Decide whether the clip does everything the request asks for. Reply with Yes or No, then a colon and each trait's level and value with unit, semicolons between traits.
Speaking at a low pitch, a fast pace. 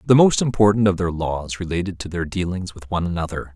Yes: very low, 90 Hz; fast, 220 wpm